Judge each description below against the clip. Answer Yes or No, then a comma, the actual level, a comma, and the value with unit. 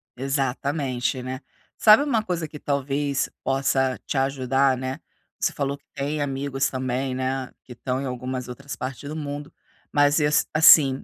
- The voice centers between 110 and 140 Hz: Yes, low, 135 Hz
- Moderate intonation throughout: No, narrow, 1.8 semitones